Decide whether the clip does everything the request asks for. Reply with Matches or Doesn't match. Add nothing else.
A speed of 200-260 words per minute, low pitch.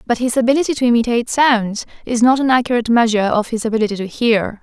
Doesn't match